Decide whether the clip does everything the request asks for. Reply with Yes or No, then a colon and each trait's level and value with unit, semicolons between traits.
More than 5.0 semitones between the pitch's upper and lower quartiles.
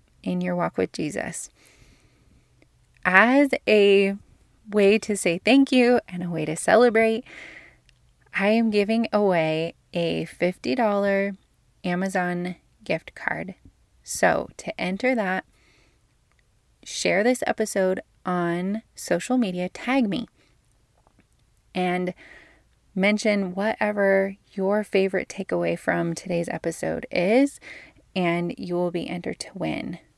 No: average, 3.4 semitones